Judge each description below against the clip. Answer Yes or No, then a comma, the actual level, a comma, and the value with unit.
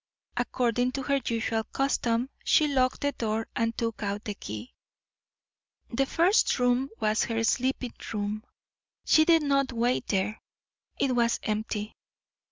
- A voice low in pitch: No, high, 235 Hz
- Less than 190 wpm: Yes, average, 140 wpm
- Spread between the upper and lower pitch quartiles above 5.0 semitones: No, average, 3.4 semitones